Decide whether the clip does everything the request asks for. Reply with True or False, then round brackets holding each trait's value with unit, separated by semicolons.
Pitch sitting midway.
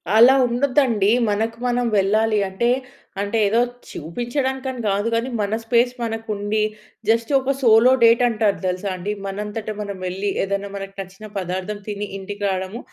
False (215 Hz)